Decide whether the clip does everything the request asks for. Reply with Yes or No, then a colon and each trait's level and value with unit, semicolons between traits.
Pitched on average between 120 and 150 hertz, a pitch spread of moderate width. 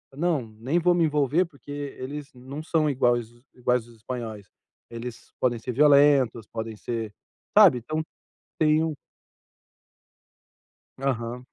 Yes: low, 135 Hz; average, 4.1 semitones